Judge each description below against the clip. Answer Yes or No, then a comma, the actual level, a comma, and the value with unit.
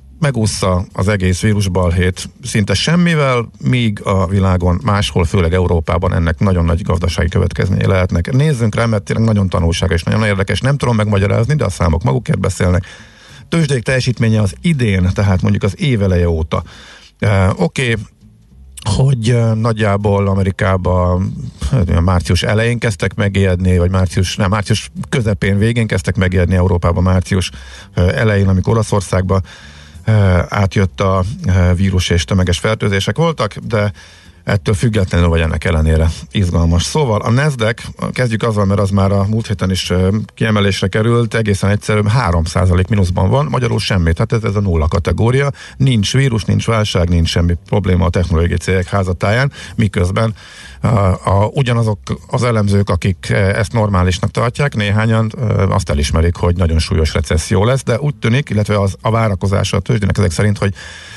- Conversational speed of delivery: Yes, average, 145 wpm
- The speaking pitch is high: No, low, 100 Hz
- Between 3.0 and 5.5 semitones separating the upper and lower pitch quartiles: Yes, average, 3.5 semitones